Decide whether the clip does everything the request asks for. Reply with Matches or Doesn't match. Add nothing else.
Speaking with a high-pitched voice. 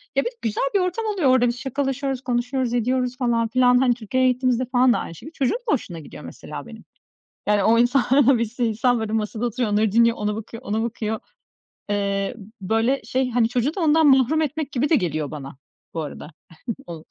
Matches